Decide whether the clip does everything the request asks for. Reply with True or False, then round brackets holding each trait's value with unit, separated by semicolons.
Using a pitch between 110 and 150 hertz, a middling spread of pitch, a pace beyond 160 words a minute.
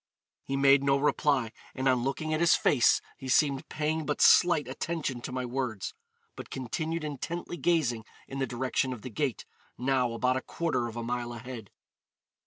True (135 Hz; 3.5 semitones; 180 wpm)